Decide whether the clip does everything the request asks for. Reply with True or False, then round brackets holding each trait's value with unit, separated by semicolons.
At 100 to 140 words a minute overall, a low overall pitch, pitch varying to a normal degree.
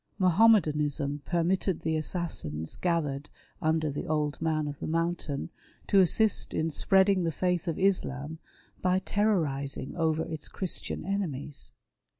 False (135 wpm; 160 Hz; 3.8 semitones)